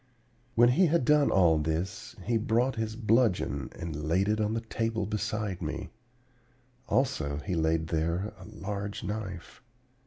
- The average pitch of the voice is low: Yes, low, 105 Hz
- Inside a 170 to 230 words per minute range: No, average, 150 wpm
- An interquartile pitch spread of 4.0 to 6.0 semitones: Yes, average, 5.1 semitones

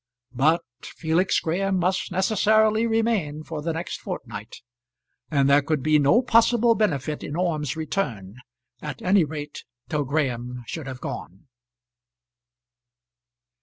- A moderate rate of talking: No, slow, 125 wpm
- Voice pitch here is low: No, medium, 160 Hz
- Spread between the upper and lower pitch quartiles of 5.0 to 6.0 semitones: Yes, average, 5.3 semitones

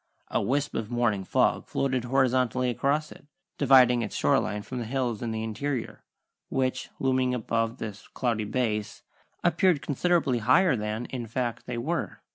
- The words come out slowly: No, average, 160 wpm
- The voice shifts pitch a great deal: No, average, 2.9 semitones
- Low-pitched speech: Yes, low, 125 Hz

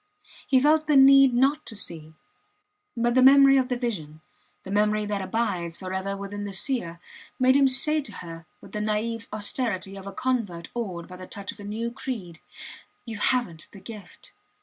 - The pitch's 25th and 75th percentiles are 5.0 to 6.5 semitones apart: Yes, average, 5.3 semitones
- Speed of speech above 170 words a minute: Yes, average, 185 wpm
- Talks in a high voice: Yes, high, 215 Hz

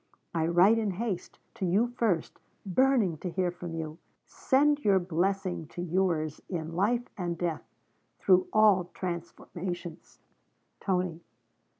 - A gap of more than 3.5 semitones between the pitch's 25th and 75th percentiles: No, average, 2.8 semitones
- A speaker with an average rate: No, slow, 125 wpm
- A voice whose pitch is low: No, medium, 180 Hz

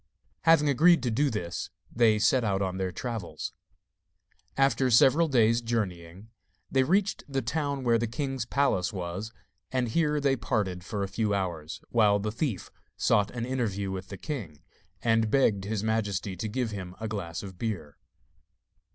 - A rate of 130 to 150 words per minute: No, average, 165 wpm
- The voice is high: No, low, 110 Hz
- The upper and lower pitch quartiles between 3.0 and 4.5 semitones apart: No, average, 5.0 semitones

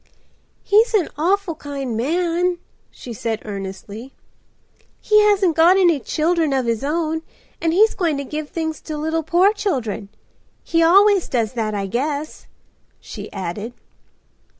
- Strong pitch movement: Yes, wide, 6.7 semitones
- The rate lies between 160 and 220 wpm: No, average, 145 wpm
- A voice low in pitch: No, very high, 310 Hz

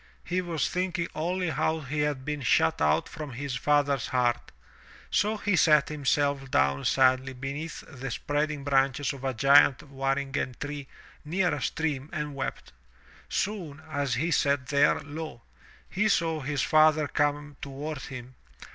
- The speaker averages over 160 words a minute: No, average, 155 wpm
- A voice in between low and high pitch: Yes, medium, 145 Hz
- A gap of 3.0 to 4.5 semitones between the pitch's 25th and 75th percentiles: No, narrow, 2.5 semitones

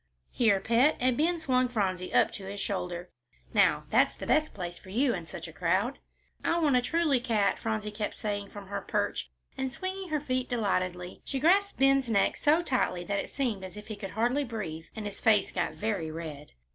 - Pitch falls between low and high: No, high, 220 Hz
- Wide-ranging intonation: Yes, wide, 5.7 semitones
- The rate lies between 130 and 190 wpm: No, fast, 205 wpm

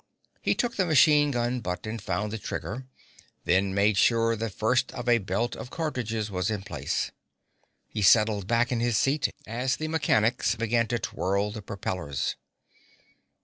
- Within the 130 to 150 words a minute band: No, average, 165 wpm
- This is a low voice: Yes, low, 115 Hz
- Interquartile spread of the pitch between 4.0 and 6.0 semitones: No, average, 3.5 semitones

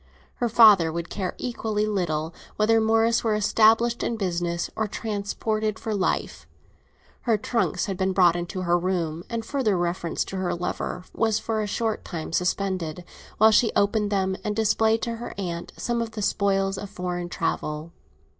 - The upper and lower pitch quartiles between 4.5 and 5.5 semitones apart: No, average, 3.8 semitones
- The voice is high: Yes, high, 200 Hz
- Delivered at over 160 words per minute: Yes, average, 170 wpm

